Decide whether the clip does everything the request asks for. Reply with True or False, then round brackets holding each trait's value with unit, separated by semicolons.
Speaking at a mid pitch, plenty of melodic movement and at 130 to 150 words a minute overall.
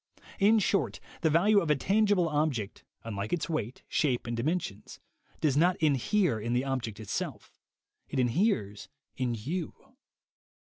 True (145 Hz; 7.2 semitones; 140 wpm)